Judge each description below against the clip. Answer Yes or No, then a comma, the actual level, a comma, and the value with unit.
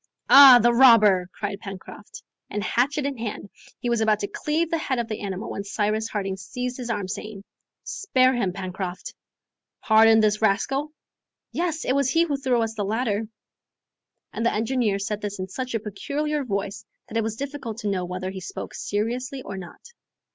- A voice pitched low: No, high, 220 Hz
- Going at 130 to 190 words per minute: Yes, average, 185 wpm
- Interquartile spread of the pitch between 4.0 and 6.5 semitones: Yes, average, 4.4 semitones